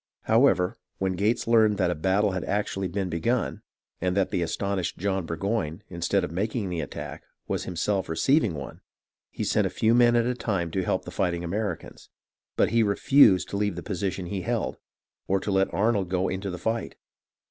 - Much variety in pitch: No, average, 3.0 semitones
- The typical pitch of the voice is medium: No, very low, 95 Hz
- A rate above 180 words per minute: Yes, average, 190 wpm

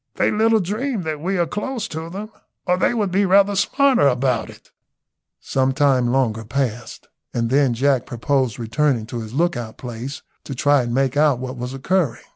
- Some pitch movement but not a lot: No, wide, 7.0 semitones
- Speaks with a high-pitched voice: No, medium, 140 Hz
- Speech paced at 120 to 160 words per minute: No, average, 185 wpm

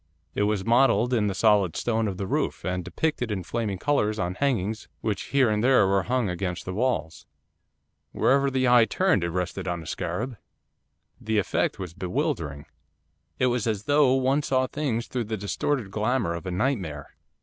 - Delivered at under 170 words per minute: No, average, 180 wpm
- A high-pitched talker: No, low, 110 Hz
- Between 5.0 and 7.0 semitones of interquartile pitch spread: Yes, wide, 5.6 semitones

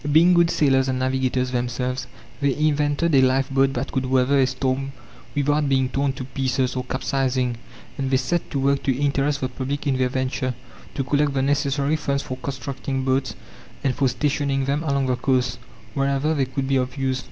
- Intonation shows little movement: Yes, narrow, 1.5 semitones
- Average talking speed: Yes, average, 190 wpm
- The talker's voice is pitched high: No, low, 135 Hz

